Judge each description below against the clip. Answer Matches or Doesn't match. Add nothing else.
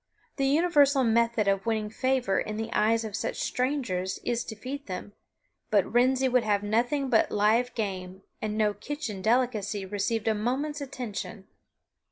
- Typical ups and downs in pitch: Matches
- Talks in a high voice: Matches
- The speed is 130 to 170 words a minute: Matches